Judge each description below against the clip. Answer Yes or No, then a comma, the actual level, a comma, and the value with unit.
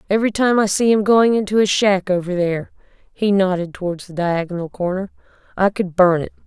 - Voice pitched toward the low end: No, high, 190 Hz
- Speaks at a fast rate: No, average, 195 wpm